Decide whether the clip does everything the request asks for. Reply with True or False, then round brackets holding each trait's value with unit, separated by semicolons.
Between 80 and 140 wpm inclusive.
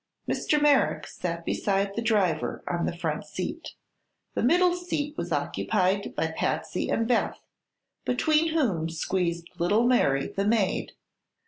True (135 wpm)